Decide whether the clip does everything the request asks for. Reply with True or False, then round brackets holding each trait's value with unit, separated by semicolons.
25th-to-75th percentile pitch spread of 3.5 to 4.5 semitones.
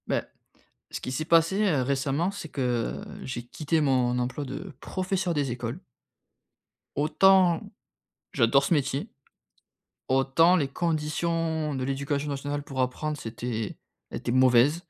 True (4.0 semitones)